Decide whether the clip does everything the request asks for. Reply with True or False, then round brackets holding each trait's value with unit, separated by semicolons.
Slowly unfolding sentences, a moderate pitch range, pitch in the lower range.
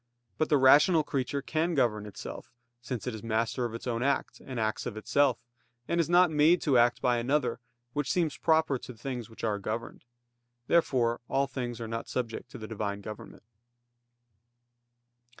False (175 wpm; 4.1 semitones; 125 Hz)